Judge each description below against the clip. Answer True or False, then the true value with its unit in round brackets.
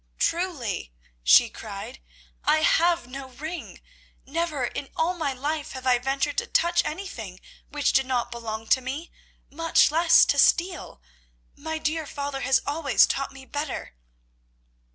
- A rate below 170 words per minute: True (145 wpm)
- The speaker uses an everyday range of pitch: True (4.0 semitones)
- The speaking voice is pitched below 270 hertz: False (285 Hz)